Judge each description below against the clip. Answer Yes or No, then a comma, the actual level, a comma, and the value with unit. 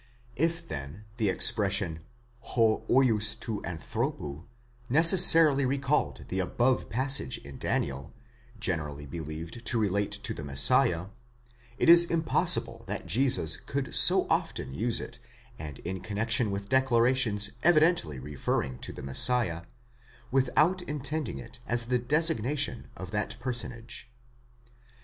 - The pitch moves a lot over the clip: Yes, wide, 7.8 semitones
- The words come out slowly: Yes, slow, 125 wpm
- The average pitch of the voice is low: Yes, low, 115 Hz